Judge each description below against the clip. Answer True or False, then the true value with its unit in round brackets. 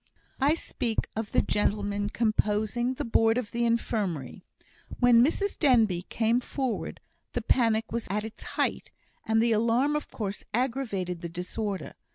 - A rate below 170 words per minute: True (150 wpm)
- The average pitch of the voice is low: False (225 Hz)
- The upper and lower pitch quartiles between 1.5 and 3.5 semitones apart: True (2.8 semitones)